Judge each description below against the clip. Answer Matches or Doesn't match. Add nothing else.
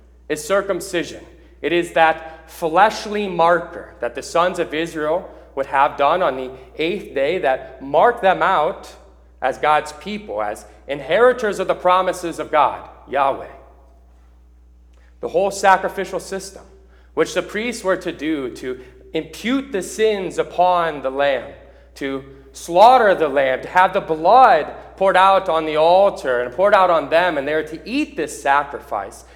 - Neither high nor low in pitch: Matches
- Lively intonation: Matches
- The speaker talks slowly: Doesn't match